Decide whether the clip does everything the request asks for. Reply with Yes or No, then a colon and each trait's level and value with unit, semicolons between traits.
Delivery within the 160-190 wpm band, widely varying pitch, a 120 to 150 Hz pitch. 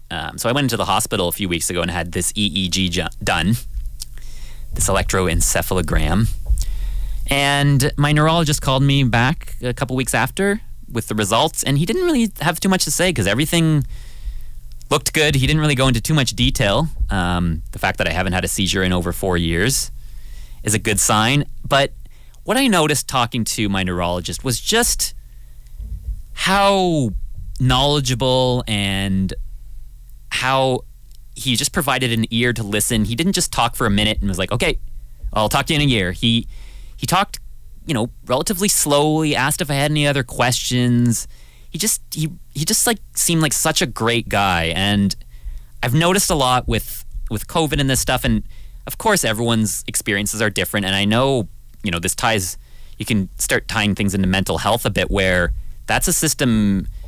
No: average, 185 wpm; wide, 7.2 semitones; low, 110 Hz